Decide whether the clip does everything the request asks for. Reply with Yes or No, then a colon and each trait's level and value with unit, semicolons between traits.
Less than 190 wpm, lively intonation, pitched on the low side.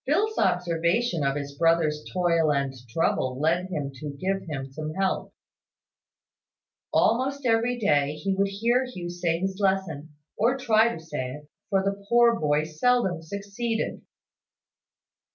No: average, 140 wpm; wide, 6.5 semitones; medium, 180 Hz